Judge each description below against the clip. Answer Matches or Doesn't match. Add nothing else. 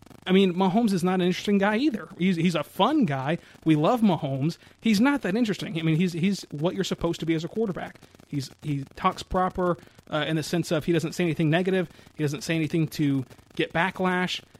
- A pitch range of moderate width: Matches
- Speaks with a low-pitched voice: Doesn't match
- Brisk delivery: Matches